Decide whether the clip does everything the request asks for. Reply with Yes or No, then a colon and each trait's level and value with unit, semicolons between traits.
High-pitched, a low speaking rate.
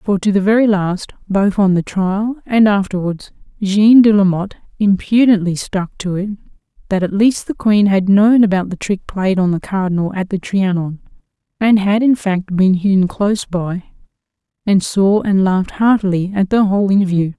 No: high, 195 Hz; average, 180 wpm